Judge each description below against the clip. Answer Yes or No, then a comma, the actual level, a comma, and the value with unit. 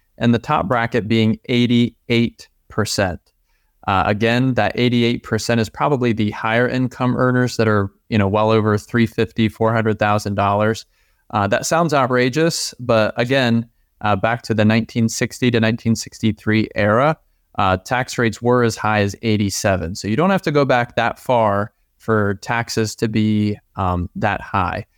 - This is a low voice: Yes, low, 115 Hz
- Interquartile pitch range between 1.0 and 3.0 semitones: Yes, narrow, 2.4 semitones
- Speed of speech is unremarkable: Yes, average, 150 wpm